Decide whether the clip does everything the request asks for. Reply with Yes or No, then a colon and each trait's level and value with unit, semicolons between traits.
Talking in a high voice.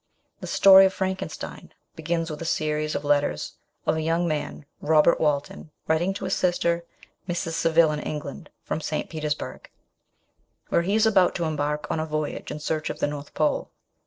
No: medium, 160 Hz